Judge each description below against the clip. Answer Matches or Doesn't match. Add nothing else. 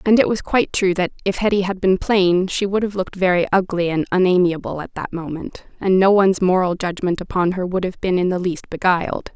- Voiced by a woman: Matches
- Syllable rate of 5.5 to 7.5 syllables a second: Matches